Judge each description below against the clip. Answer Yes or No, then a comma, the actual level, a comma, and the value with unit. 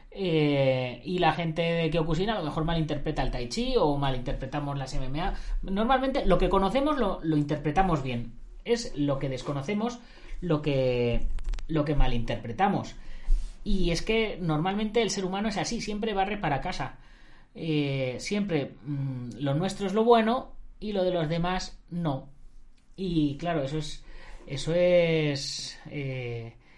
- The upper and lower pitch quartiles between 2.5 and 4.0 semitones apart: No, wide, 5.6 semitones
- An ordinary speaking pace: Yes, average, 150 wpm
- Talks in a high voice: No, medium, 160 Hz